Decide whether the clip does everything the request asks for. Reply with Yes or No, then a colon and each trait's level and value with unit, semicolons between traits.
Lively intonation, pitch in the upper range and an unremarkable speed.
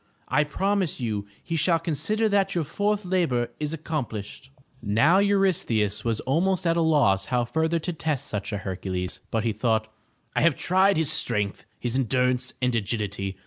No: wide, 7.4 semitones; low, 135 Hz; average, 175 wpm